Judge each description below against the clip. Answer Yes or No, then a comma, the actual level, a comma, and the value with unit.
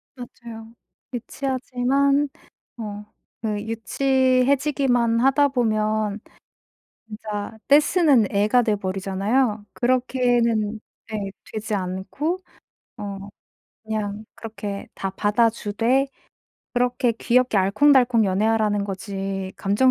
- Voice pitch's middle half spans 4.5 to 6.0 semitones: No, average, 3.6 semitones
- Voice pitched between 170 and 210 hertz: No, high, 225 Hz